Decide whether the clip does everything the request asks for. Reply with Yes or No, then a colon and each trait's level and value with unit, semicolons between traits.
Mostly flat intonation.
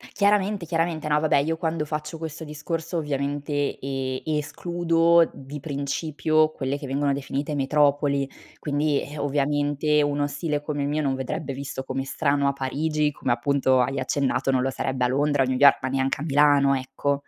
Yes: narrow, 1.9 semitones